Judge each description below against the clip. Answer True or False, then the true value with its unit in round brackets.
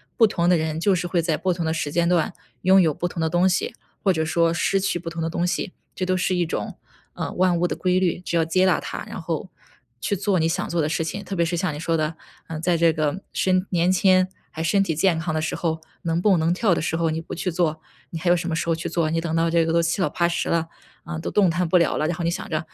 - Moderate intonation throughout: False (2.0 semitones)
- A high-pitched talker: False (170 Hz)